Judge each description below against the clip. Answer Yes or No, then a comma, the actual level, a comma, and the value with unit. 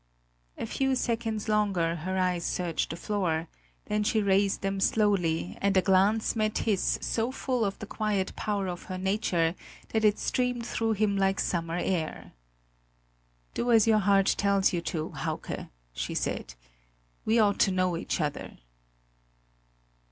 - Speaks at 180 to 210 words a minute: No, average, 155 wpm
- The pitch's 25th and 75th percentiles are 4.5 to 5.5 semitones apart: No, average, 3.1 semitones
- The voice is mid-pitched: No, high, 195 Hz